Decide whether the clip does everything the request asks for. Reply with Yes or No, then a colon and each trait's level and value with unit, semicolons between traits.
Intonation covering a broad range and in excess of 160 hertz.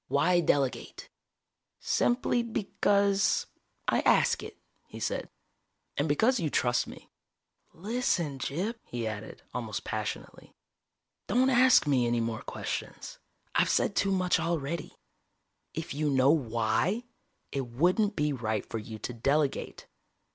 No: wide, 8.0 semitones; medium, 150 Hz